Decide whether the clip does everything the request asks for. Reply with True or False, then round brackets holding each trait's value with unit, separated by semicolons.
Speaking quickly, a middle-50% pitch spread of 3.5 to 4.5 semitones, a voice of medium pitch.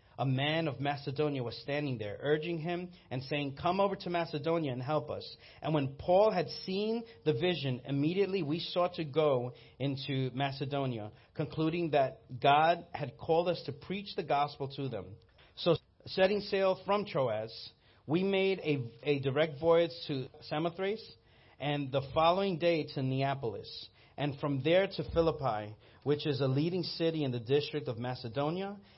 False (160 wpm; 4.1 semitones; 150 Hz)